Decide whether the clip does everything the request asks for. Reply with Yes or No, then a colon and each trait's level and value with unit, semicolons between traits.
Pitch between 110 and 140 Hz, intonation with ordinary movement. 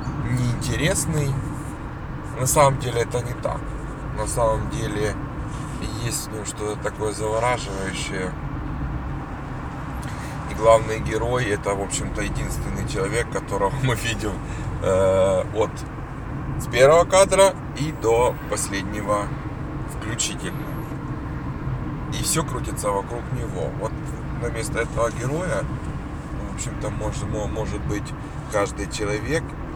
Yes: low, 135 Hz; average, 4.5 semitones